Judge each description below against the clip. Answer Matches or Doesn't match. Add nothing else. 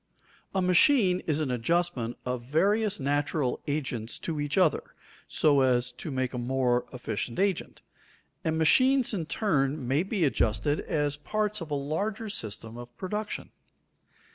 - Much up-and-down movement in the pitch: Matches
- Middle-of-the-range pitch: Matches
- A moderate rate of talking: Matches